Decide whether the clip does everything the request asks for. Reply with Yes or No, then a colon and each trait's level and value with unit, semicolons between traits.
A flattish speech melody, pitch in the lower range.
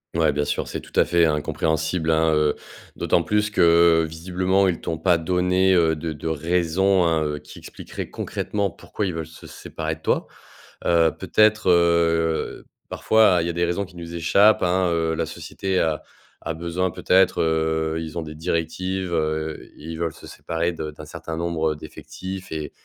Yes: narrow, 2.1 semitones; very low, 85 Hz